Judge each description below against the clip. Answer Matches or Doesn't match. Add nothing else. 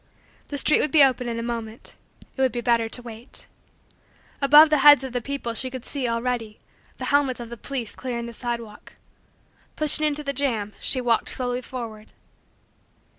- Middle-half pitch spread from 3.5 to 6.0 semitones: Doesn't match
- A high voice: Matches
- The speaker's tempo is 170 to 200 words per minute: Matches